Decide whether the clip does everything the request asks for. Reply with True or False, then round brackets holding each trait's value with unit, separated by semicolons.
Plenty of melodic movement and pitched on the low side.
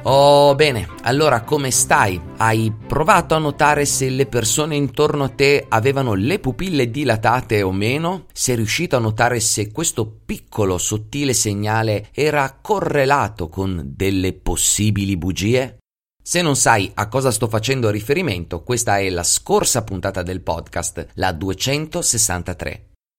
True (6.2 semitones; 115 Hz)